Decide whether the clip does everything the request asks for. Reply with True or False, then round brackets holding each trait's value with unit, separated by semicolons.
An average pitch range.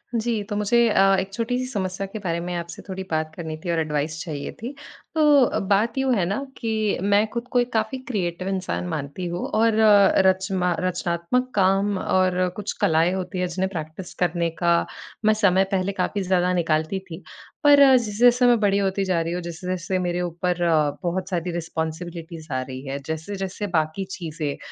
True (3.4 semitones)